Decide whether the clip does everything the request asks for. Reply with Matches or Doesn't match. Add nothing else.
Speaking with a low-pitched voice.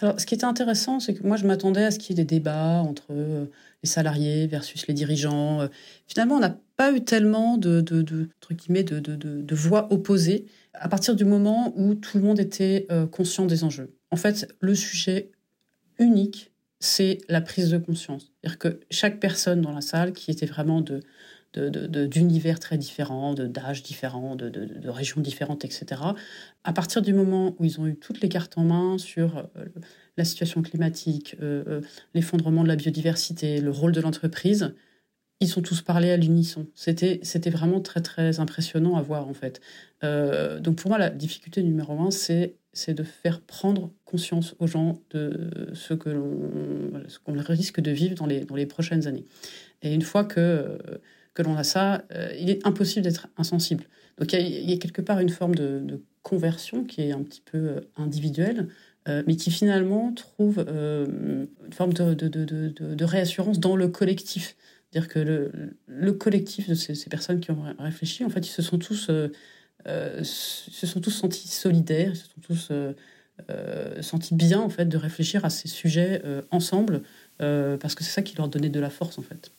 Doesn't match